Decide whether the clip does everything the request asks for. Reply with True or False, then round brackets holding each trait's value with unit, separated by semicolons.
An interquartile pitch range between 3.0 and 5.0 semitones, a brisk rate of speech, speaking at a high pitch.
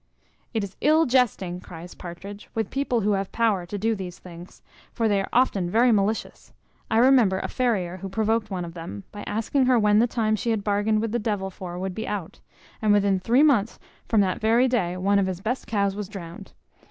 True (3.3 semitones; 215 wpm; 205 Hz)